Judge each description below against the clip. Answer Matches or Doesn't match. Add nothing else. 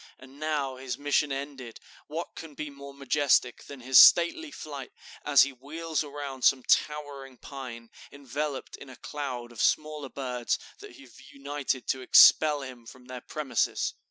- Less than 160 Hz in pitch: Matches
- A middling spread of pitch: Doesn't match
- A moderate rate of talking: Matches